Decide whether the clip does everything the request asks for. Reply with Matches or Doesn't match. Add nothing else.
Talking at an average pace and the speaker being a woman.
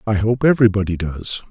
Doesn't match